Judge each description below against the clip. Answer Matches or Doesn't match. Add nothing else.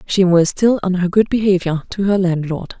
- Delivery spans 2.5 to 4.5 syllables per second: Doesn't match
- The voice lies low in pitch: Doesn't match